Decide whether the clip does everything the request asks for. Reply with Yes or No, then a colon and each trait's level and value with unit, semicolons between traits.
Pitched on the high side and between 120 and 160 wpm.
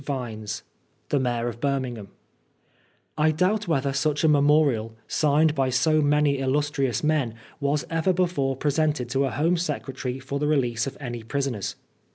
No: medium, 140 Hz; average, 155 wpm